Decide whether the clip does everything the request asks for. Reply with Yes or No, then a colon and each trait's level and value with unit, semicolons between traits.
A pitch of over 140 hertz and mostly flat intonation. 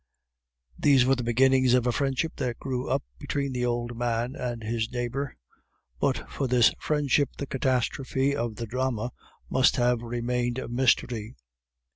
No: low, 125 Hz; narrow, 1.8 semitones